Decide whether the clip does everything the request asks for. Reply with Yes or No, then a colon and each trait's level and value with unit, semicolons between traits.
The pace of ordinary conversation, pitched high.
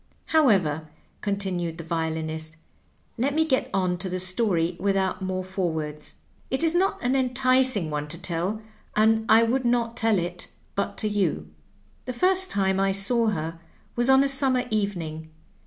Yes: average, 170 wpm; high, 195 Hz